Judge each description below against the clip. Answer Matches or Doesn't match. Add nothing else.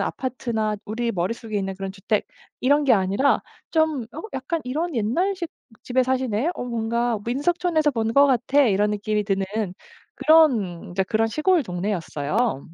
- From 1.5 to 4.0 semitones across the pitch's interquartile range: Doesn't match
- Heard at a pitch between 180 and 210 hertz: Doesn't match